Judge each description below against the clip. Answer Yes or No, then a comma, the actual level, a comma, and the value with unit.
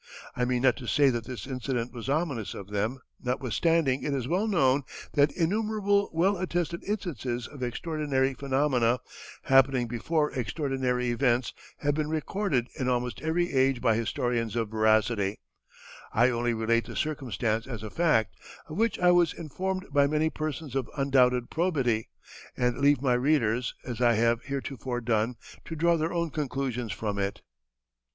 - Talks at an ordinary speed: Yes, average, 160 wpm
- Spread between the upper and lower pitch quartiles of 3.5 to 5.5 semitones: Yes, average, 4.5 semitones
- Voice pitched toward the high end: No, low, 130 Hz